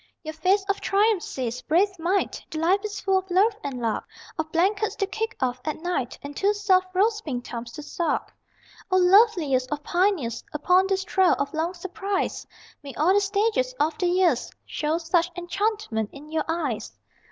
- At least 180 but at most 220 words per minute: Yes, average, 185 wpm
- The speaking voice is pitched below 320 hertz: No, very high, 355 Hz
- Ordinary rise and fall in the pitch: Yes, average, 4.7 semitones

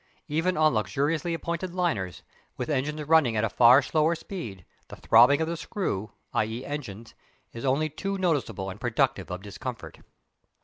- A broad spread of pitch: Yes, wide, 6.4 semitones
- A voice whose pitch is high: No, medium, 140 Hz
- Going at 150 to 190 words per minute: Yes, average, 160 wpm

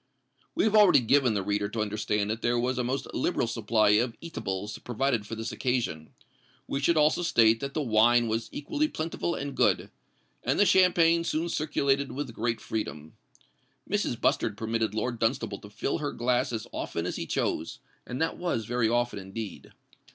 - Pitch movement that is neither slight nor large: Yes, average, 4.3 semitones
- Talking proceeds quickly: No, average, 180 wpm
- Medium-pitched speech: No, low, 120 Hz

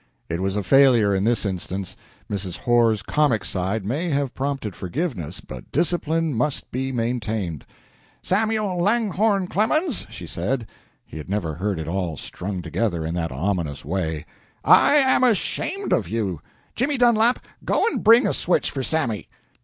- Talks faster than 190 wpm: No, average, 155 wpm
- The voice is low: Yes, low, 115 Hz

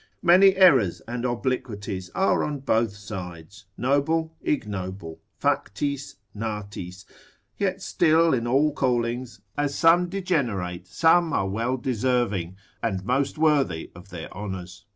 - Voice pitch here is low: Yes, low, 120 Hz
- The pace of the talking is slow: Yes, slow, 120 wpm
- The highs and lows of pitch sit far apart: Yes, wide, 7.3 semitones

